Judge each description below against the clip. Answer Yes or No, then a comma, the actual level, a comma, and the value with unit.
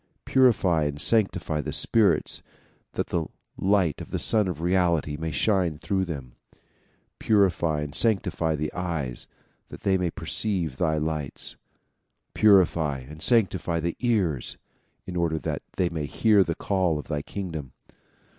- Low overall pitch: Yes, very low, 85 Hz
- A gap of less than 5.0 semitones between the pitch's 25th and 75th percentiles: Yes, average, 4.0 semitones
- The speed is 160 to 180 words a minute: No, average, 145 wpm